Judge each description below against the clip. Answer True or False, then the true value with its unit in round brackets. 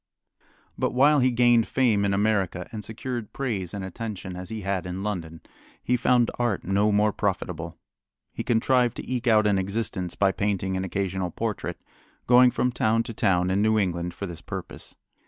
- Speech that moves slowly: False (180 wpm)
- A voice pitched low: True (105 Hz)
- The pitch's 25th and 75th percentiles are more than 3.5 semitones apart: True (4.0 semitones)